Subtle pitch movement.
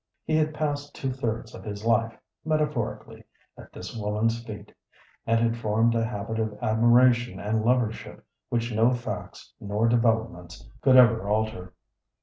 Yes: narrow, 2.0 semitones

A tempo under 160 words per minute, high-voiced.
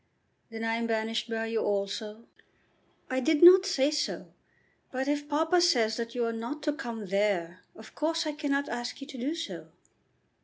No: average, 185 wpm; high, 240 Hz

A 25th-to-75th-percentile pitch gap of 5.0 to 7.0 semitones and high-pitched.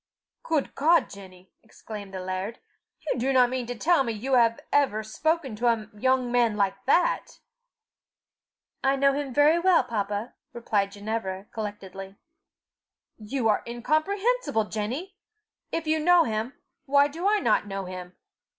Yes: wide, 5.6 semitones; high, 235 Hz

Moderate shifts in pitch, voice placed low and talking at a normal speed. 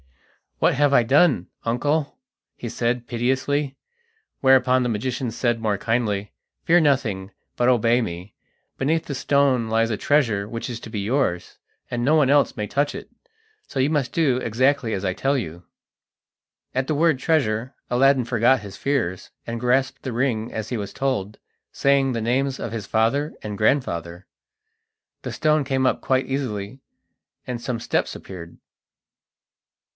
Yes: average, 3.8 semitones; low, 125 Hz; average, 160 wpm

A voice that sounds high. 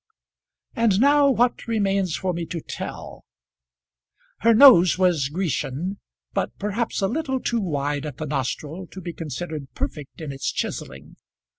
No: medium, 180 Hz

